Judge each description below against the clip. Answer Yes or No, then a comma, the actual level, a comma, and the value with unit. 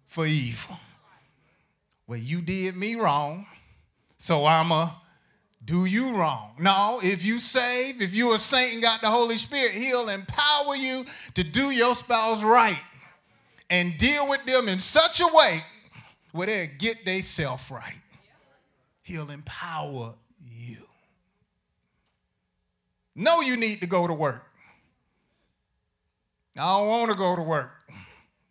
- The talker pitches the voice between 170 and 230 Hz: Yes, medium, 185 Hz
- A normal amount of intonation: No, wide, 8.4 semitones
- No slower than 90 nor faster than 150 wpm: Yes, slow, 135 wpm